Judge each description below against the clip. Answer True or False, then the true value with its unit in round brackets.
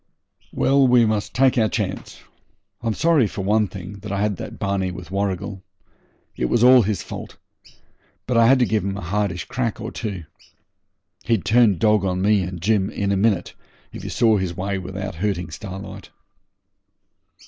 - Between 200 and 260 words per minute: False (180 wpm)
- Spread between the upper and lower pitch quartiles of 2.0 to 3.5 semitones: True (2.9 semitones)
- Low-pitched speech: True (100 Hz)